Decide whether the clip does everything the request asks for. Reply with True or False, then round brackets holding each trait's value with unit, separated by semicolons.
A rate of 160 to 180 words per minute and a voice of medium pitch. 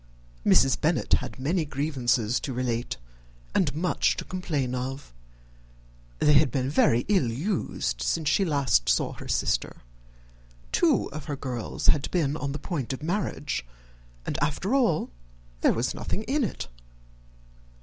False (150 wpm; 145 Hz)